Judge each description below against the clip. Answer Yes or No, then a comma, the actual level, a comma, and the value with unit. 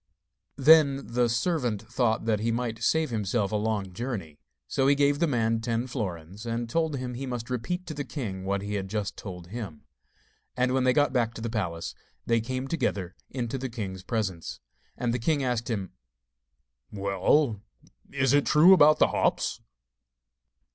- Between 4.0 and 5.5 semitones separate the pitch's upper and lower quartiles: Yes, average, 4.3 semitones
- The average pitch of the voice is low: Yes, low, 115 Hz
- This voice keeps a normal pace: Yes, average, 175 wpm